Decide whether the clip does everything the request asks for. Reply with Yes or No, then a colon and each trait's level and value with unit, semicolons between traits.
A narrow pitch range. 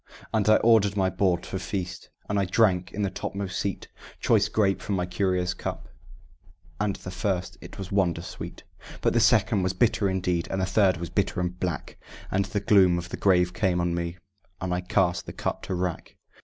Yes: narrow, 1.9 semitones